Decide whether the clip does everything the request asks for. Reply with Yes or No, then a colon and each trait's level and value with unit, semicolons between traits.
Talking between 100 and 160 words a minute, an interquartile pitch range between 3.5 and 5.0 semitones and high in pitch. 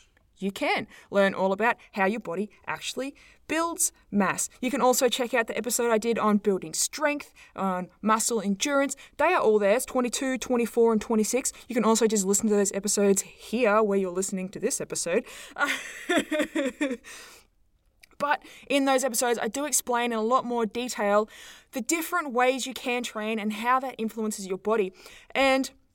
No: average, 175 wpm; average, 4.0 semitones; high, 235 Hz